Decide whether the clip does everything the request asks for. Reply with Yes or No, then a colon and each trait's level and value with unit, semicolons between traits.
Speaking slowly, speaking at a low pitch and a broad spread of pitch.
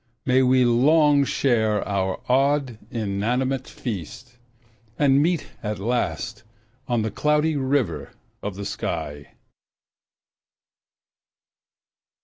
No: slow, 95 wpm; low, 125 Hz; average, 4.8 semitones